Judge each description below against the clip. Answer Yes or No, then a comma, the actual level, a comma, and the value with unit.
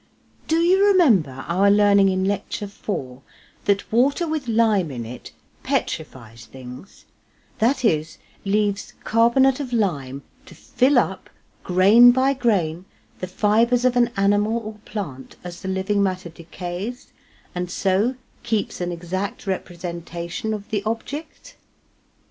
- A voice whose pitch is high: Yes, high, 200 Hz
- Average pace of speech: No, slow, 130 wpm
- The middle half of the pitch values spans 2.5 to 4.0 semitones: No, average, 5.1 semitones